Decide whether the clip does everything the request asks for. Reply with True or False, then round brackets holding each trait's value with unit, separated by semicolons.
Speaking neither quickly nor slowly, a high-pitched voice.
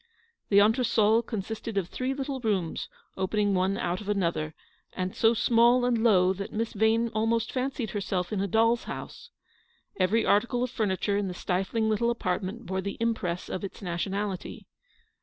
True (170 wpm; 210 Hz)